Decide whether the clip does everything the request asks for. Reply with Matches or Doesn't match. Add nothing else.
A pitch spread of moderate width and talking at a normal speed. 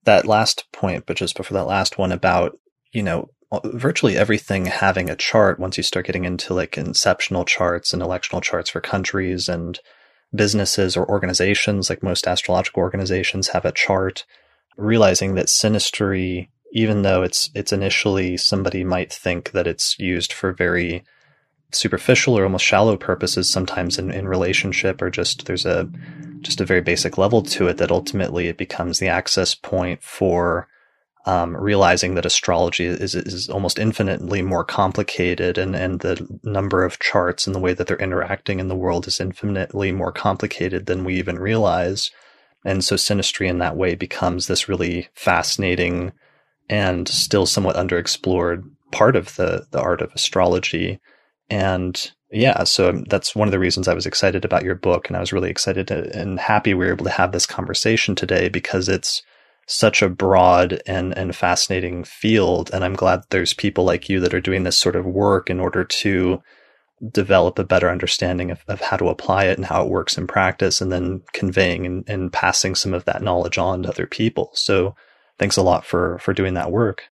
Doesn't match